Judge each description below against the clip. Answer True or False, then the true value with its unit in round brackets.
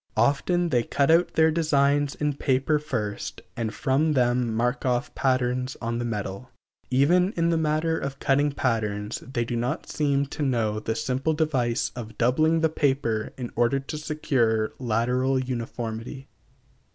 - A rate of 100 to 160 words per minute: True (155 wpm)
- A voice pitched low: True (130 Hz)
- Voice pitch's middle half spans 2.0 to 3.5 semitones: False (3.9 semitones)